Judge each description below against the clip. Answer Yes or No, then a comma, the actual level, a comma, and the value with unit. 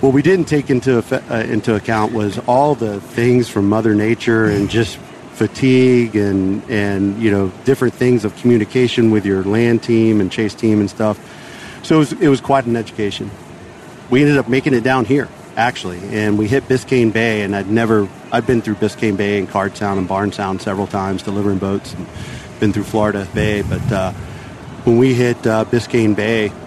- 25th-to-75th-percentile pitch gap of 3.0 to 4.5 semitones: Yes, average, 3.3 semitones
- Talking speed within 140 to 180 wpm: No, average, 195 wpm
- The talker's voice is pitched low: Yes, low, 110 Hz